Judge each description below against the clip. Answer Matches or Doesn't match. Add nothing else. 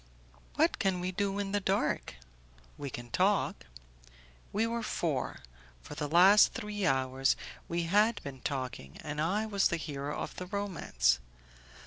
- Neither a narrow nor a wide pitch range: Doesn't match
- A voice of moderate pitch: Matches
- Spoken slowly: Doesn't match